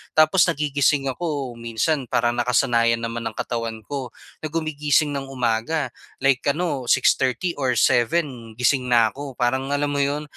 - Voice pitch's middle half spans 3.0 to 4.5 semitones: Yes, average, 3.4 semitones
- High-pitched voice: No, low, 135 Hz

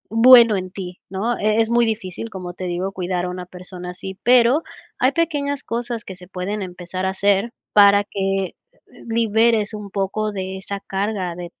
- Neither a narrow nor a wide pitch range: Yes, average, 3.6 semitones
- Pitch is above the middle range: Yes, high, 200 Hz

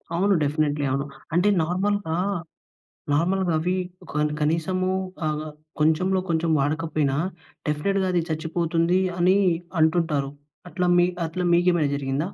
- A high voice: No, medium, 165 Hz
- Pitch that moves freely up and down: No, average, 3.2 semitones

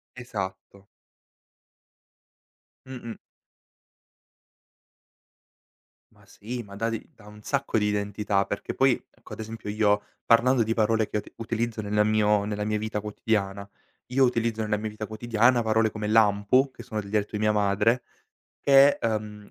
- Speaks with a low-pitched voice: Yes, low, 110 Hz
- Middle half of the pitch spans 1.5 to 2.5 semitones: Yes, narrow, 1.8 semitones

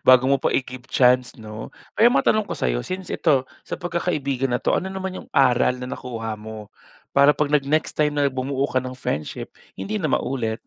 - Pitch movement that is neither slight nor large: Yes, average, 3.5 semitones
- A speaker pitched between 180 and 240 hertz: No, low, 135 Hz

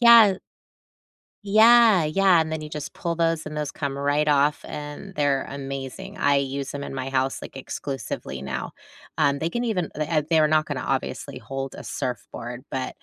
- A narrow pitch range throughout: No, average, 3.6 semitones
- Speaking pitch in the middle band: Yes, medium, 150 Hz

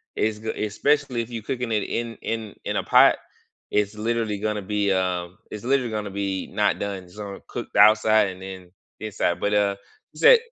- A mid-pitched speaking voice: No, low, 105 Hz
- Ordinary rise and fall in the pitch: No, narrow, 2.2 semitones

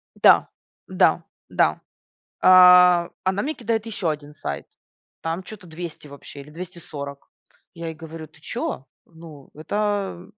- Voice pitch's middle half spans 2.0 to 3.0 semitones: No, average, 3.4 semitones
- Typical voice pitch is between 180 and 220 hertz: No, medium, 165 Hz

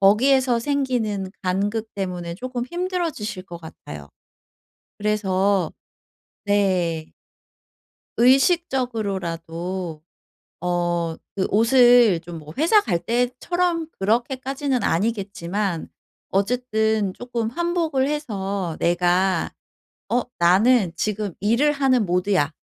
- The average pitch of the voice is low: No, high, 210 Hz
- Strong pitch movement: Yes, wide, 5.7 semitones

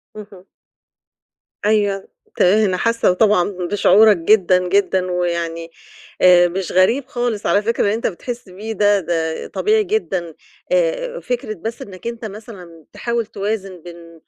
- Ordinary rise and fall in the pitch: Yes, average, 4.0 semitones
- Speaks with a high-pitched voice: Yes, high, 200 Hz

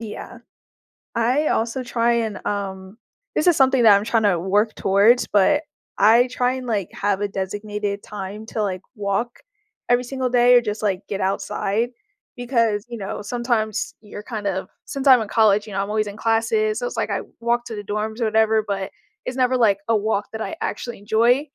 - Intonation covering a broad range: No, average, 2.7 semitones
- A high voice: Yes, high, 220 Hz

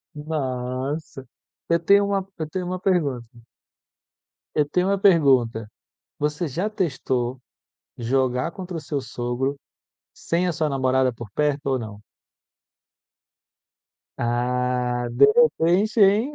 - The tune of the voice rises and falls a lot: Yes, wide, 6.0 semitones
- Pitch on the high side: No, medium, 145 Hz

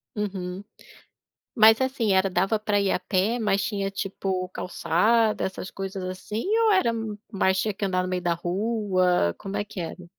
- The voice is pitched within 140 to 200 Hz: Yes, high, 195 Hz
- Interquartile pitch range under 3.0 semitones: Yes, narrow, 2.5 semitones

